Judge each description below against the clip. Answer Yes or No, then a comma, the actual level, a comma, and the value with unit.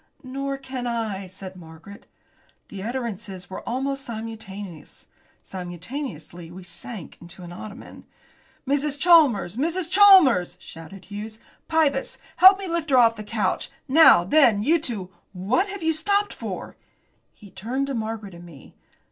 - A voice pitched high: Yes, high, 225 Hz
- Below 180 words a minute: Yes, average, 145 wpm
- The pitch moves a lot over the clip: Yes, wide, 6.9 semitones